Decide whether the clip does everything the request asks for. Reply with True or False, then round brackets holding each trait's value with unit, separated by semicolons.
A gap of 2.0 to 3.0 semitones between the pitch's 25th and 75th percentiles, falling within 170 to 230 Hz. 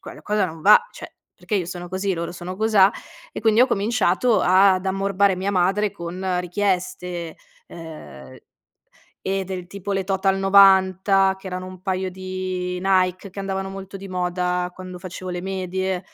False (1.4 semitones; 185 Hz)